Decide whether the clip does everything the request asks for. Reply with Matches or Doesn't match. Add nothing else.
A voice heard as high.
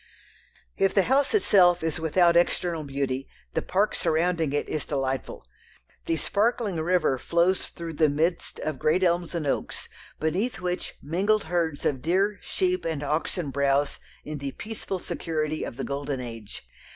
Doesn't match